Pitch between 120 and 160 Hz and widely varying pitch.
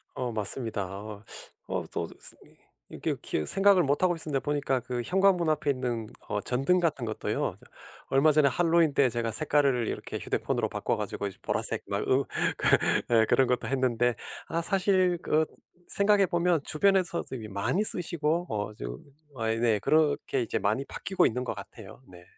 Yes: low, 135 Hz; wide, 6.7 semitones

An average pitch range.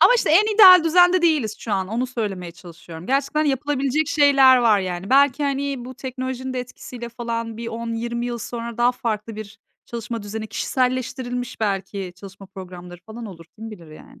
Yes: average, 4.2 semitones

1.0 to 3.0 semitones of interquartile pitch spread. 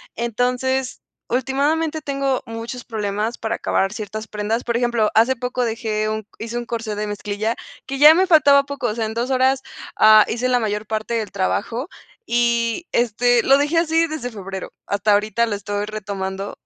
No: average, 3.4 semitones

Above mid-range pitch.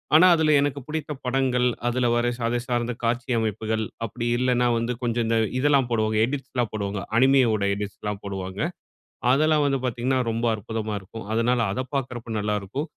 No: low, 120 Hz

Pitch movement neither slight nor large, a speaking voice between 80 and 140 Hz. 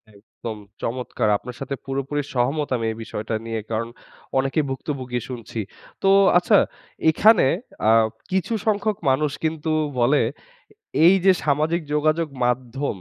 Yes: average, 4.5 semitones; low, 135 Hz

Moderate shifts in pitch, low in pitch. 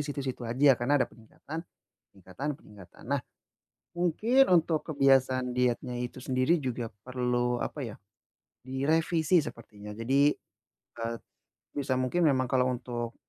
Yes: average, 3.0 semitones; low, 130 Hz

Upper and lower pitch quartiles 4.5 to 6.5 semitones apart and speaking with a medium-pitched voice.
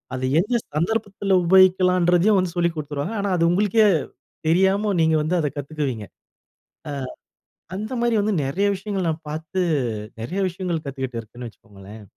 Yes: average, 4.9 semitones; medium, 175 Hz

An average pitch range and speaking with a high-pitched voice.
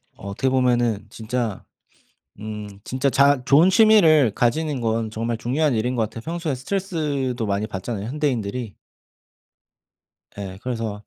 No: average, 4.5 semitones; low, 125 Hz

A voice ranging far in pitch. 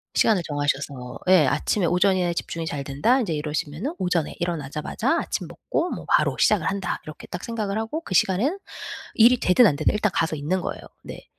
Yes: wide, 5.8 semitones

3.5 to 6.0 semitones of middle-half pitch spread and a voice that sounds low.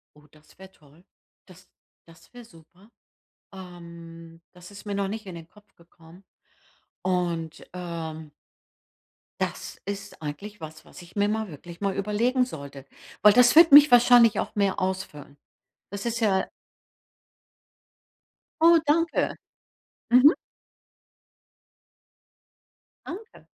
No: average, 4.6 semitones; high, 190 Hz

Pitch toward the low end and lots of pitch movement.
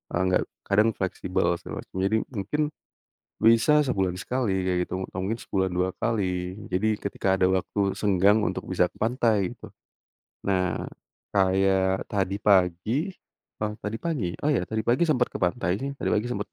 No: low, 100 Hz; average, 3.2 semitones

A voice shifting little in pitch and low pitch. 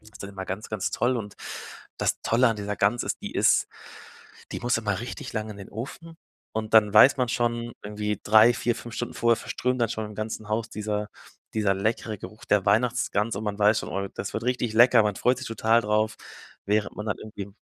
Yes: narrow, 2.0 semitones; low, 110 Hz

